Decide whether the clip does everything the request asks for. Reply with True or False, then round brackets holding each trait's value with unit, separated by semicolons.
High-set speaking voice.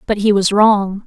True (205 Hz)